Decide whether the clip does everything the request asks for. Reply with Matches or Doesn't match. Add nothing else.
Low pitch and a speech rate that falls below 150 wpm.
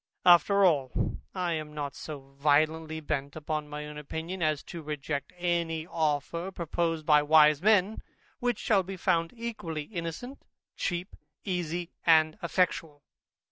Doesn't match